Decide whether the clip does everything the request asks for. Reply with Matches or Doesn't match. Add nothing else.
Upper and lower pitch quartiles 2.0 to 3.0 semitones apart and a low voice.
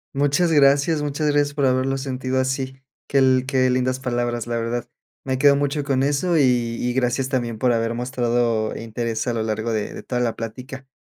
Matches